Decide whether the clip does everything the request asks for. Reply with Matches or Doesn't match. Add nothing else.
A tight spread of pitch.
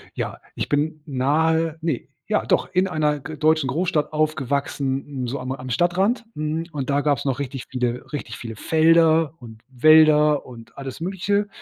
Doesn't match